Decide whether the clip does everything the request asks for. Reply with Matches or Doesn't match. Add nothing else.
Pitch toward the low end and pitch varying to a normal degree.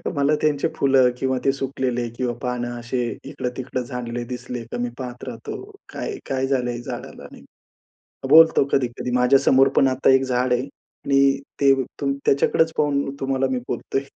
Doesn't match